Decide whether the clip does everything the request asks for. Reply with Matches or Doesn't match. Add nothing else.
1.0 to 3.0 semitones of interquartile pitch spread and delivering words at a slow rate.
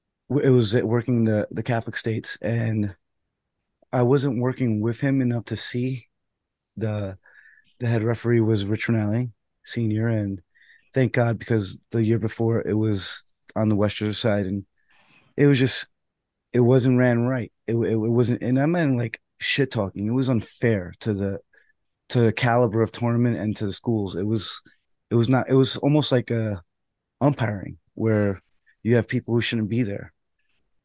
Doesn't match